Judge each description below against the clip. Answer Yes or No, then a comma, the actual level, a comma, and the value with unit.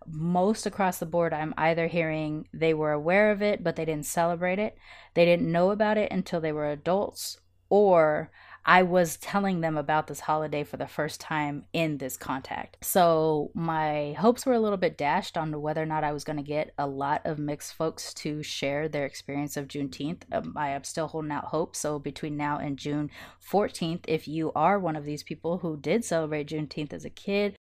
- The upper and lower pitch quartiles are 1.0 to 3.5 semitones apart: Yes, average, 2.8 semitones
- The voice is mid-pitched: Yes, medium, 155 Hz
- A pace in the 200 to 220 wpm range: Yes, fast, 205 wpm